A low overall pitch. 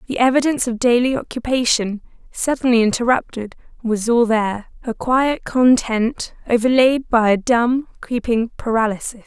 No: high, 240 Hz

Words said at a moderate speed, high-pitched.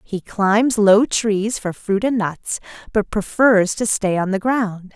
Yes: average, 180 wpm; high, 210 Hz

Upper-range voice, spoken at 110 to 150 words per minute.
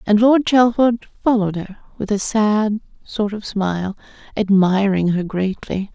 Yes: high, 205 Hz; average, 140 wpm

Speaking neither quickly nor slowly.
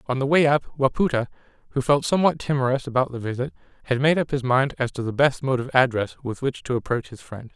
No: fast, 240 wpm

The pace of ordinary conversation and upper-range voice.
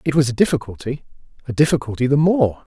No: average, 155 wpm; low, 135 Hz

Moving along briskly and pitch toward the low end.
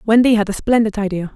No: fast, 220 wpm; high, 215 Hz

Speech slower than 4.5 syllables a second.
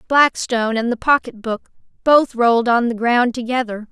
No: 5.0 syllables/s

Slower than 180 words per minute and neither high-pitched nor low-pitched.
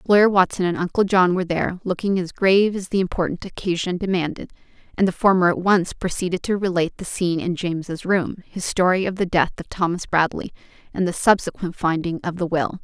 No: average, 200 wpm; medium, 180 Hz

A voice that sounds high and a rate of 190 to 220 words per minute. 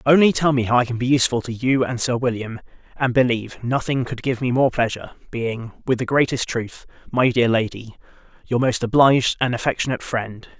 No: low, 125 Hz; average, 200 wpm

